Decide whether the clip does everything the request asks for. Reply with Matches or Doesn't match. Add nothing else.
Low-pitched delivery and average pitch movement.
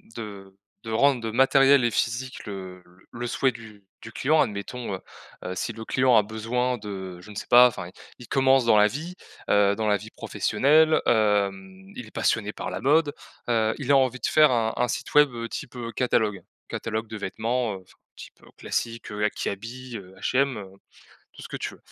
Matches